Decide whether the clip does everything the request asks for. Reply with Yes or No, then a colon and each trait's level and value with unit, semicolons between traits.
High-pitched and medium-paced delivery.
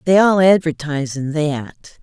No: medium, 160 Hz; average, 150 wpm